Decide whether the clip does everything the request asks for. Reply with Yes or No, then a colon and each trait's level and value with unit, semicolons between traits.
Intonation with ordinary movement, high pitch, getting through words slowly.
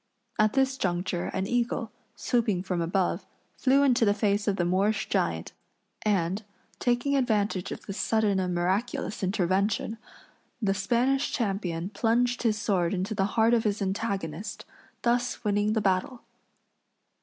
No: average, 3.6 semitones; high, 205 Hz; average, 145 wpm